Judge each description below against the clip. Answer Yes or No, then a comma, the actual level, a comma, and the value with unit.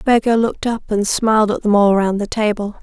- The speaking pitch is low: No, high, 215 Hz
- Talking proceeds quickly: Yes, fast, 235 wpm